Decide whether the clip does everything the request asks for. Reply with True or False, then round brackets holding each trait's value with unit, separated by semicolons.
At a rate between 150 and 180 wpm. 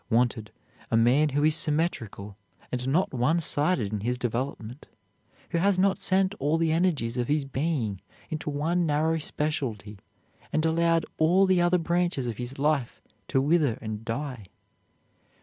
True (155 wpm)